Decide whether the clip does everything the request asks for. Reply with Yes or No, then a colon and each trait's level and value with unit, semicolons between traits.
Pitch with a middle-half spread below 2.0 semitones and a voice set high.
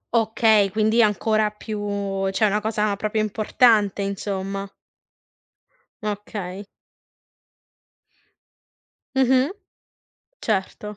Yes: narrow, 1.5 semitones; high, 210 Hz